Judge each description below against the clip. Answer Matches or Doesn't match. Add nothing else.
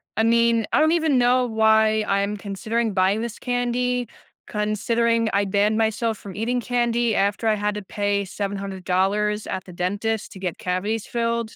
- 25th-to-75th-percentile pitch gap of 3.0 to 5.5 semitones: Doesn't match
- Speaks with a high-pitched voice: Matches